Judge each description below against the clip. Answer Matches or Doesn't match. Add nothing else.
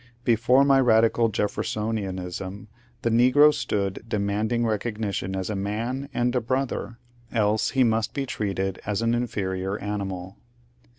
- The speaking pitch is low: Matches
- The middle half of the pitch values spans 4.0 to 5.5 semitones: Doesn't match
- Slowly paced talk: Matches